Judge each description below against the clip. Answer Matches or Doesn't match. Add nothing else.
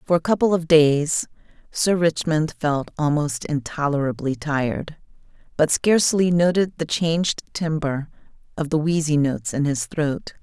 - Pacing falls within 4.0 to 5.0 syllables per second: Matches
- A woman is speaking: Matches